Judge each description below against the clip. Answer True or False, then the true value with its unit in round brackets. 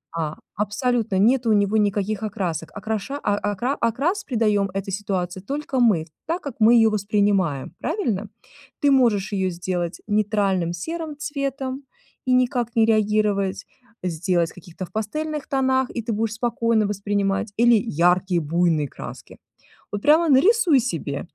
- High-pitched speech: True (215 Hz)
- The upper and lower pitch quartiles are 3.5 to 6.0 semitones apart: True (4.8 semitones)